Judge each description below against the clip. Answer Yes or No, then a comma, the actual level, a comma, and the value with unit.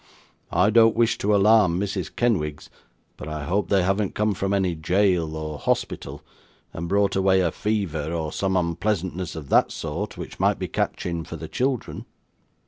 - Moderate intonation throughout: Yes, average, 3.9 semitones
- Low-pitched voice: Yes, very low, 95 Hz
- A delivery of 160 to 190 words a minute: Yes, average, 170 wpm